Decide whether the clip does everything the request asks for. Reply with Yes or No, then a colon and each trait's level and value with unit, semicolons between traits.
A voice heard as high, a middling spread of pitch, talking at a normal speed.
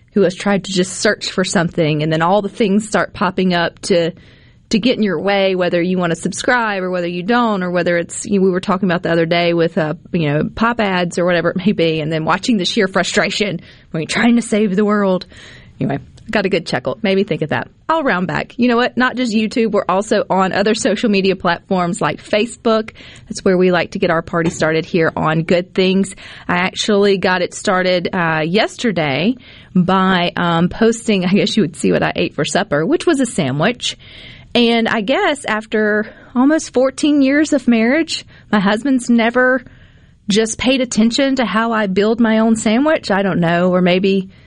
No: high, 200 Hz; average, 4.3 semitones; fast, 215 wpm